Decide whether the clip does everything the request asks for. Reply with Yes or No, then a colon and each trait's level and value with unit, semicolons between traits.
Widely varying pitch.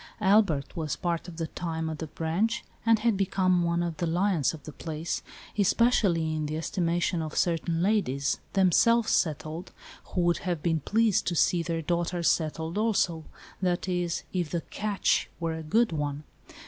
No: average, 2.9 semitones